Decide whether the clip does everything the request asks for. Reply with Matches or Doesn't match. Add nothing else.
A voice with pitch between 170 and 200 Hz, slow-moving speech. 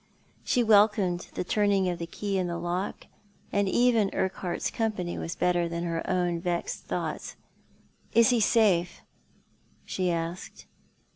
Doesn't match